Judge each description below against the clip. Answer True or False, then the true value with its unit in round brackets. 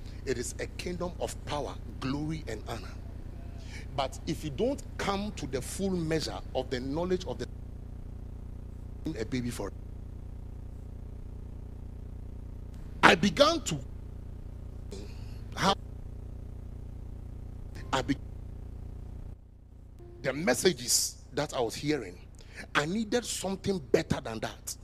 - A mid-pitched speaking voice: False (105 Hz)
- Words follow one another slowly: True (100 wpm)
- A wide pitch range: True (5.9 semitones)